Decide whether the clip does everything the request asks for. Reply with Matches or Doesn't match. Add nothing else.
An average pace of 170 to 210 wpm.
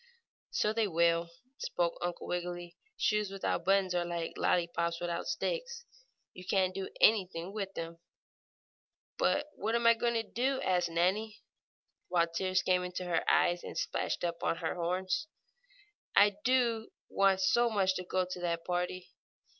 Doesn't match